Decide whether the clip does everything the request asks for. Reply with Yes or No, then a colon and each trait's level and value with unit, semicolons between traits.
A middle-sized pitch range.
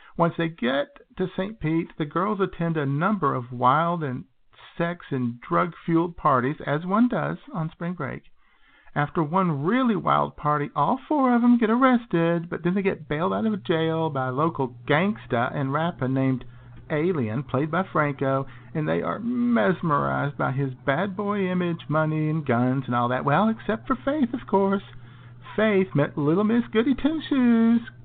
No: wide, 6.8 semitones